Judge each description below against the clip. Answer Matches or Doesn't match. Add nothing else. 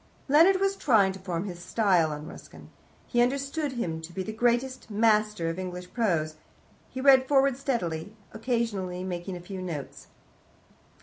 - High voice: Matches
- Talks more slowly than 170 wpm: Matches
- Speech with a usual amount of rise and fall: Doesn't match